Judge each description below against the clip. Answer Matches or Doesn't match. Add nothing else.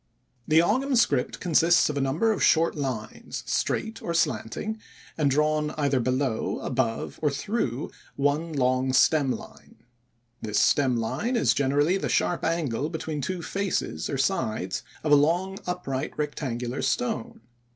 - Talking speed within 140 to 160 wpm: Matches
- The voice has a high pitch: Doesn't match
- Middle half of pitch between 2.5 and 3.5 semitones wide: Doesn't match